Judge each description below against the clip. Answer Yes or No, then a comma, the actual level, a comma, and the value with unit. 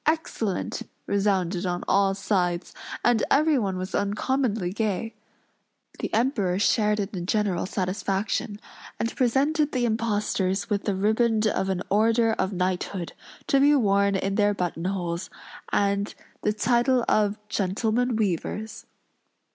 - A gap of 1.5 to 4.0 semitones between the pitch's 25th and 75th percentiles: Yes, average, 3.0 semitones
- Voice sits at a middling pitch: No, high, 205 Hz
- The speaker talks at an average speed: No, slow, 130 wpm